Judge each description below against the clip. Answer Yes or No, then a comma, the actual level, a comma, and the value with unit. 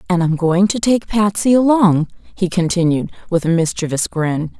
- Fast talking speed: No, average, 170 wpm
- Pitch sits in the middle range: Yes, medium, 180 Hz